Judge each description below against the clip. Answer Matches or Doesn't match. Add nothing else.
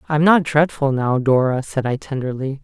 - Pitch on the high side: Doesn't match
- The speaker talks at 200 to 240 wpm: Matches